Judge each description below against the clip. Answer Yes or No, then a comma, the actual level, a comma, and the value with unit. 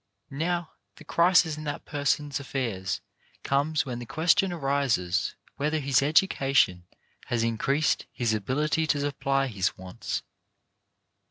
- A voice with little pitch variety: No, average, 4.4 semitones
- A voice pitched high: No, medium, 140 Hz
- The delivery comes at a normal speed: No, slow, 120 wpm